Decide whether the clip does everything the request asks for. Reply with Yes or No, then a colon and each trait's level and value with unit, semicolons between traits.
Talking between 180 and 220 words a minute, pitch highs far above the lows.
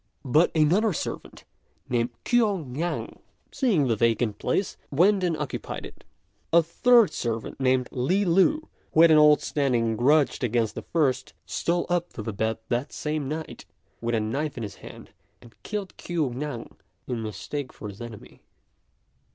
No: average, 160 wpm; wide, 6.4 semitones